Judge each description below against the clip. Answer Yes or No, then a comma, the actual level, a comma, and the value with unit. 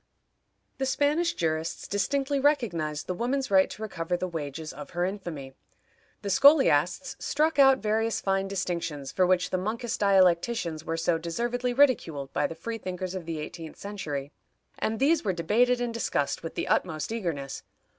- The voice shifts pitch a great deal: Yes, wide, 6.5 semitones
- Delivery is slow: No, average, 165 wpm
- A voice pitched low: No, high, 190 Hz